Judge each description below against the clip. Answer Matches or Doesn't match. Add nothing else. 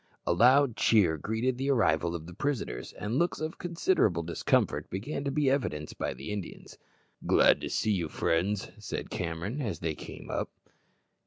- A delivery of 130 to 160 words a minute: Doesn't match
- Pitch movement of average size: Doesn't match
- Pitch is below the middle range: Matches